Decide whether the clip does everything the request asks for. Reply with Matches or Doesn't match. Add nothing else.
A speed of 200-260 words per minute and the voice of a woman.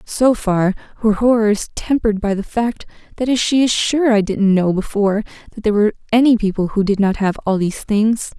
Matches